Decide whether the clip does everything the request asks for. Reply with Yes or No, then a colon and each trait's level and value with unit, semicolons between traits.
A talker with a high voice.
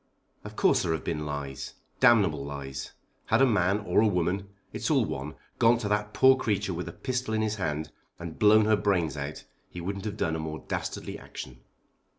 No: very low, 95 Hz